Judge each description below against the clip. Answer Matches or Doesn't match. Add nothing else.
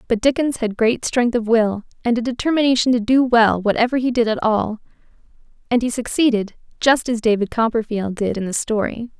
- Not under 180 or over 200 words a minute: Matches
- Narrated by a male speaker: Doesn't match